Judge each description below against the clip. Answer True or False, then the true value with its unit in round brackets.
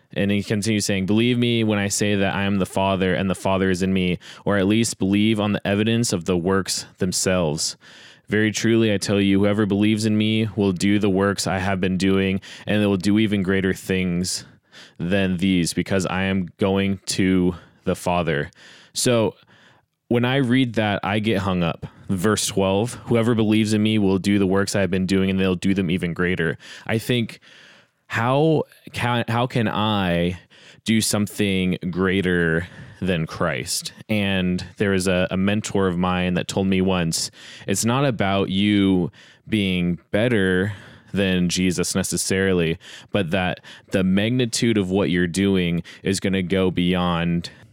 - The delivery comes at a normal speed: True (175 wpm)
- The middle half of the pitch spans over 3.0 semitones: False (2.4 semitones)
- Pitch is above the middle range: False (95 Hz)